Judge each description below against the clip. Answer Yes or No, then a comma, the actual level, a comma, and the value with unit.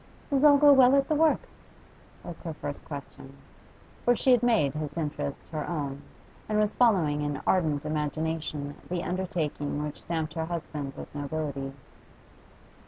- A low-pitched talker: No, medium, 155 Hz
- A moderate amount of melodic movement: No, wide, 5.7 semitones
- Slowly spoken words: No, average, 155 wpm